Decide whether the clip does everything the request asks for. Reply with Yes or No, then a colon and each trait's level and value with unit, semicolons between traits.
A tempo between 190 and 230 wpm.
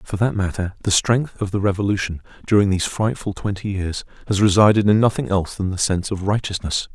Yes: average, 200 wpm